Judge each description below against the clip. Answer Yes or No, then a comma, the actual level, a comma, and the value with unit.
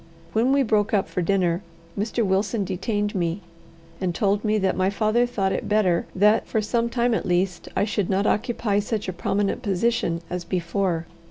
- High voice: Yes, high, 200 Hz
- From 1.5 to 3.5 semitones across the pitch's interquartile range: Yes, average, 2.7 semitones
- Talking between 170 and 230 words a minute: Yes, average, 185 wpm